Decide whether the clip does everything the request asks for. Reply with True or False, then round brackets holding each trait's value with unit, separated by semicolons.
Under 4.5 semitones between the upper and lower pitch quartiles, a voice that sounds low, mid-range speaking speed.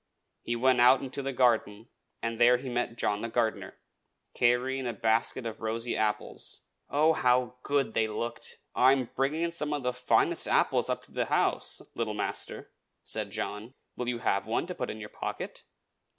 True (2.5 semitones; 120 Hz; 180 wpm)